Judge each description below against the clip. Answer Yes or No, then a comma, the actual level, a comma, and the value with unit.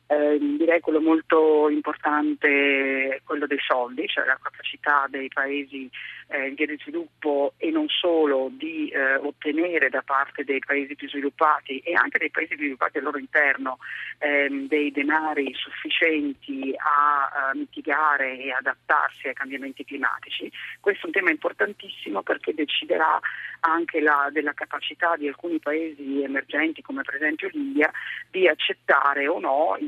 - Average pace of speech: Yes, average, 150 wpm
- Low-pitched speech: No, medium, 145 Hz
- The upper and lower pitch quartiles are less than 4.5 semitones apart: Yes, narrow, 2.6 semitones